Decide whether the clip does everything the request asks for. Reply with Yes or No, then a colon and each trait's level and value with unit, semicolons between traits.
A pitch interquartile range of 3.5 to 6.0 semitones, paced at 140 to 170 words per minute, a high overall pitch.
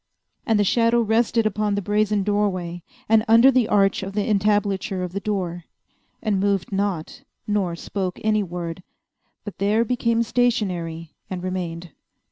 No: average, 2.9 semitones; average, 150 wpm; high, 200 Hz